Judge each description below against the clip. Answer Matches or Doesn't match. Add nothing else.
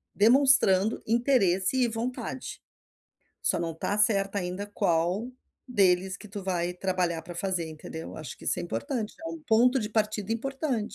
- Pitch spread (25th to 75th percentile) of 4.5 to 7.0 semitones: Matches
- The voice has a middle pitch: Doesn't match